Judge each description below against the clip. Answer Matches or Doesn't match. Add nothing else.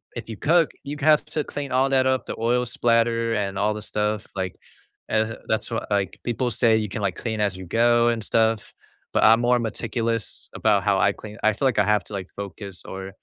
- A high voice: Doesn't match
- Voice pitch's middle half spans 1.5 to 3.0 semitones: Matches